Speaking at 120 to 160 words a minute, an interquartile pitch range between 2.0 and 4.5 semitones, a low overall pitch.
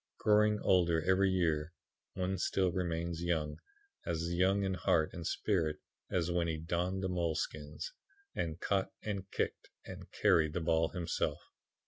Yes: average, 145 wpm; narrow, 2.5 semitones; very low, 85 Hz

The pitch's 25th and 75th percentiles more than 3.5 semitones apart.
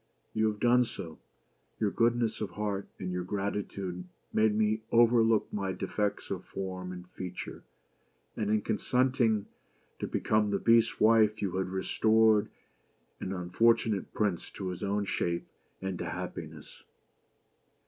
No: average, 2.8 semitones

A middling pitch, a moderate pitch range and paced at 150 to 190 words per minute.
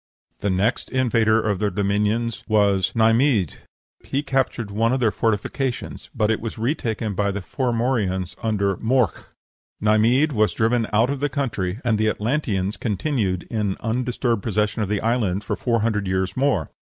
No: low, 110 Hz; average, 3.1 semitones; average, 160 wpm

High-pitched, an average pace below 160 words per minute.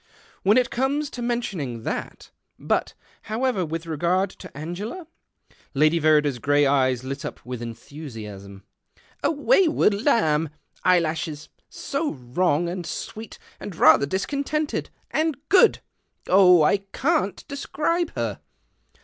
No: medium, 175 Hz; slow, 135 wpm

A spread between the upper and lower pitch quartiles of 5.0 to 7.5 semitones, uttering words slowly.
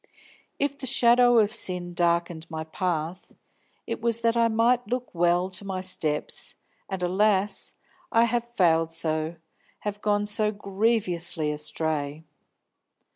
Yes: wide, 5.4 semitones; slow, 130 wpm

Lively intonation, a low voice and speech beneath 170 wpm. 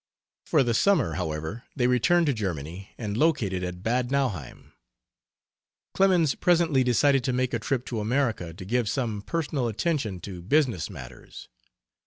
Yes: wide, 6.4 semitones; low, 120 Hz; average, 150 wpm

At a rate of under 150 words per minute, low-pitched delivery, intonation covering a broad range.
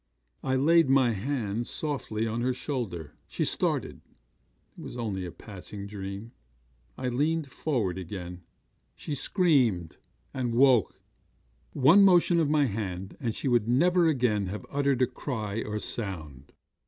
Yes: average, 140 wpm; low, 120 Hz; wide, 5.9 semitones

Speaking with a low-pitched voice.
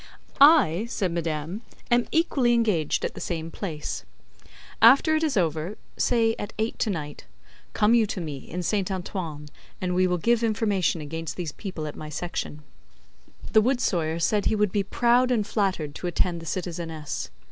No: medium, 185 Hz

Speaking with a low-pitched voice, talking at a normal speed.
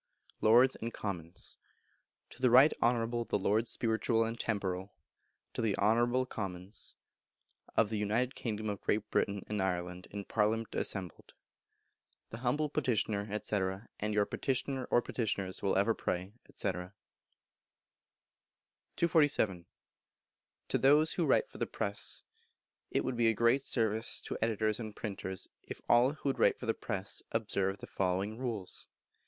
Yes: low, 110 Hz; average, 150 wpm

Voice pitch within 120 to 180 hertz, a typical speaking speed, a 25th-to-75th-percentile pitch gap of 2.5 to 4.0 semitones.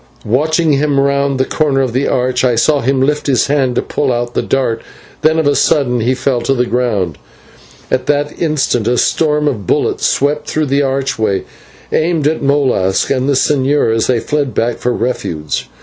Yes: low, 135 Hz; average, 195 wpm; average, 3.1 semitones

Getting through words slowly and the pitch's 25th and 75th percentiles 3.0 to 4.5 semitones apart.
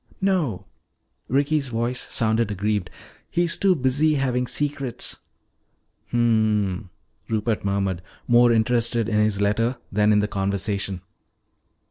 Yes: slow, 115 wpm; average, 3.5 semitones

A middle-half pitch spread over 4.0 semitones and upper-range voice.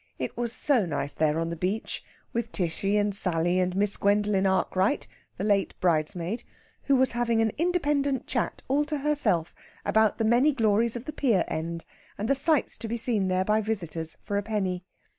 Yes: average, 4.6 semitones; high, 210 Hz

